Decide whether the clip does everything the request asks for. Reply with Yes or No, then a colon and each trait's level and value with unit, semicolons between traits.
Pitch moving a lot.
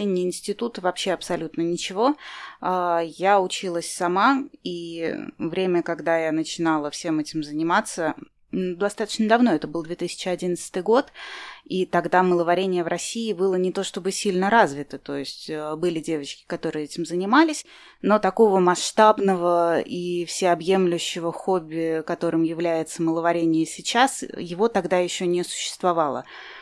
No: average, 2.9 semitones